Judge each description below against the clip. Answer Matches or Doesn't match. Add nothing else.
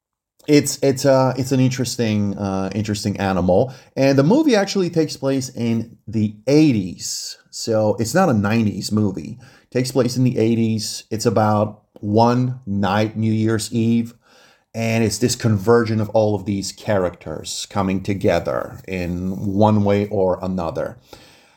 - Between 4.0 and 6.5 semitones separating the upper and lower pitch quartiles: Doesn't match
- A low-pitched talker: Matches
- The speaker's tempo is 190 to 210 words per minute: Doesn't match